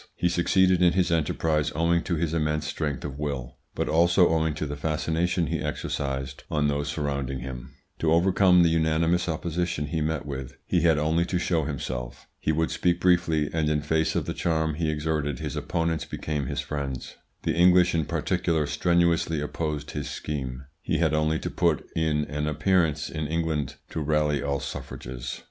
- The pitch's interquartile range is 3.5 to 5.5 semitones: No, narrow, 2.4 semitones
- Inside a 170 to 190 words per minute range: Yes, average, 180 wpm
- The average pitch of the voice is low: Yes, very low, 80 Hz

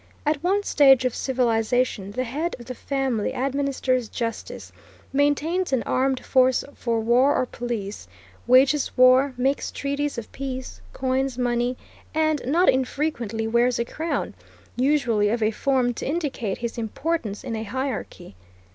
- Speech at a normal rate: Yes, average, 145 wpm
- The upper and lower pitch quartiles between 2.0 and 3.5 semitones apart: Yes, average, 2.9 semitones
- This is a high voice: Yes, very high, 255 Hz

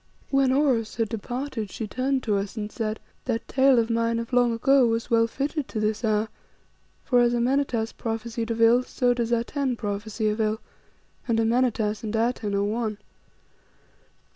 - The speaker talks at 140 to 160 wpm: No, average, 170 wpm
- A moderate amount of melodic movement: No, narrow, 2.2 semitones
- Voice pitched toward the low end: No, high, 230 Hz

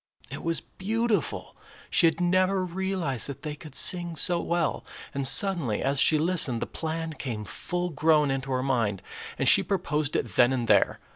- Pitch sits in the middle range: Yes, medium, 155 Hz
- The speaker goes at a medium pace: Yes, average, 180 wpm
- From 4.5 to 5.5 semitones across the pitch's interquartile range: Yes, average, 4.8 semitones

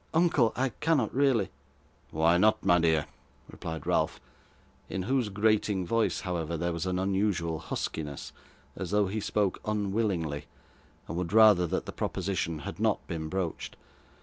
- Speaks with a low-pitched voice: Yes, very low, 95 Hz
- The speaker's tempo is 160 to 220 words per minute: No, average, 150 wpm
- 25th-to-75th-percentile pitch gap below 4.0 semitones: No, average, 4.3 semitones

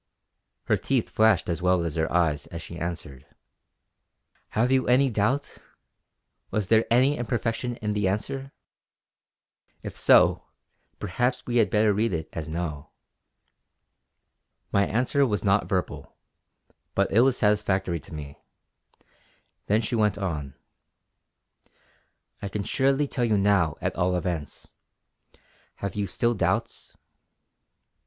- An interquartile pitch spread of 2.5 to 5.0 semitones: No, wide, 5.4 semitones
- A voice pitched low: Yes, low, 105 Hz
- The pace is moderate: No, slow, 130 wpm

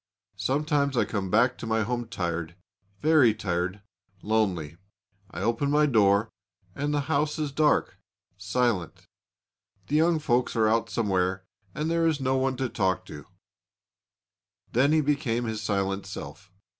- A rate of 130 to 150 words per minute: Yes, average, 145 wpm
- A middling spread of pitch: No, wide, 6.5 semitones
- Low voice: Yes, low, 115 Hz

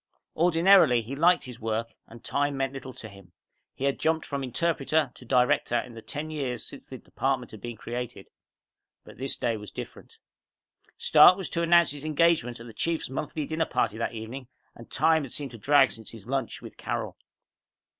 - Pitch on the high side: No, low, 135 Hz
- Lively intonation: No, average, 5.0 semitones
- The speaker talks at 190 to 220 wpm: Yes, average, 195 wpm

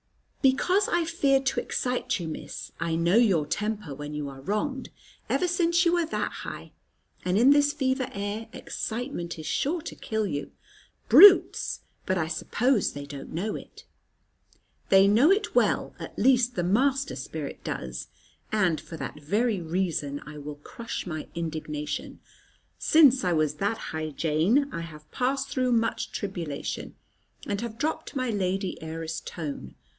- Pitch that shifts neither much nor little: No, wide, 8.7 semitones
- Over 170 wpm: No, average, 160 wpm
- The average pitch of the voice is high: Yes, high, 200 Hz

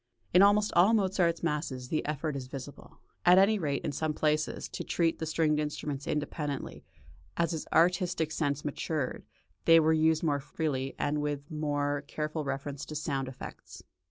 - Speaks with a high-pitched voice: No, medium, 150 Hz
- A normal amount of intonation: No, narrow, 2.3 semitones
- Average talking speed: Yes, average, 165 wpm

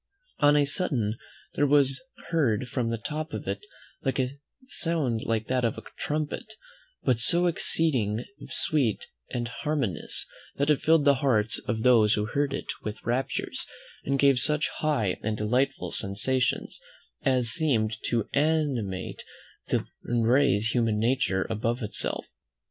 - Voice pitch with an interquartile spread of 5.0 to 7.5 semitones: No, average, 4.6 semitones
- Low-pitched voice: Yes, low, 125 Hz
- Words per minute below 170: Yes, average, 140 wpm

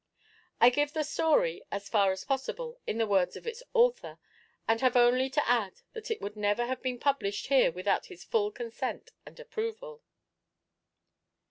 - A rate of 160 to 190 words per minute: Yes, average, 170 wpm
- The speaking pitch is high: Yes, very high, 265 Hz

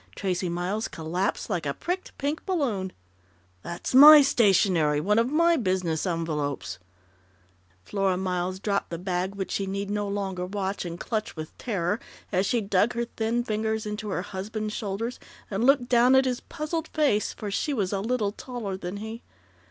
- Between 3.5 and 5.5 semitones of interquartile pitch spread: Yes, average, 4.4 semitones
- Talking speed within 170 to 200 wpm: Yes, average, 175 wpm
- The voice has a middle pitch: No, high, 200 Hz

